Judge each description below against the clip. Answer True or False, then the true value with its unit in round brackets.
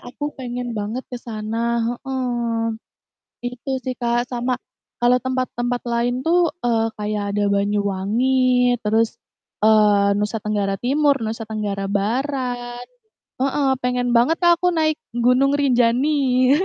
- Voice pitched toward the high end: True (240 Hz)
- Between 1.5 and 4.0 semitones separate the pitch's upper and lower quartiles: True (2.8 semitones)